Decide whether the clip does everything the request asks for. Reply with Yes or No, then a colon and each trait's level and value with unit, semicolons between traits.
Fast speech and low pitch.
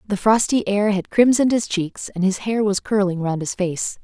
No: fast, 225 wpm; high, 200 Hz